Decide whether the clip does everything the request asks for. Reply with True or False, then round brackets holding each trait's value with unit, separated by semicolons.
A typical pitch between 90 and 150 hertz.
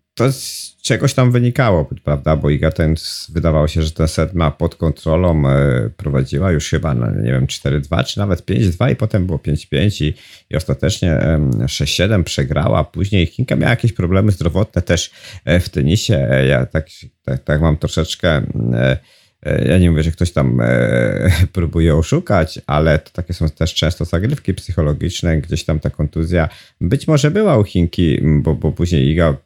False (80 Hz)